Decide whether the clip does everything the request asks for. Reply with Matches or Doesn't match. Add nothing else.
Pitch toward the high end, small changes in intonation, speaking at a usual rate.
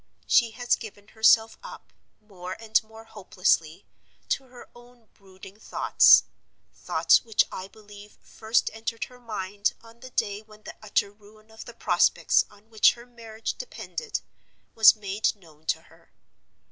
Matches